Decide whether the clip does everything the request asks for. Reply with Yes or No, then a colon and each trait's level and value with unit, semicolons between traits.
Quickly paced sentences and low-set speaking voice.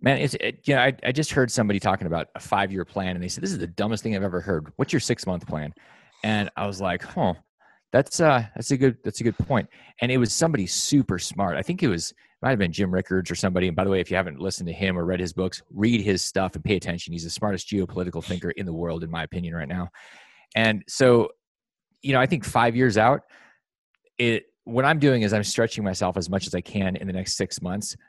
Yes: fast, 260 wpm; low, 100 Hz